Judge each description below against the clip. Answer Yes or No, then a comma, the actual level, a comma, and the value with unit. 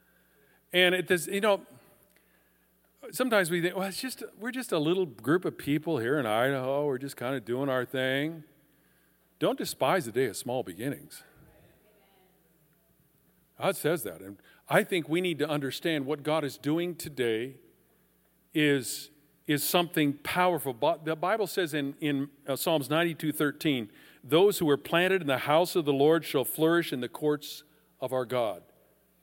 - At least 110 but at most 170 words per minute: Yes, average, 165 wpm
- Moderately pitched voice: Yes, medium, 150 Hz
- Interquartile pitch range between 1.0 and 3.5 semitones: No, average, 4.0 semitones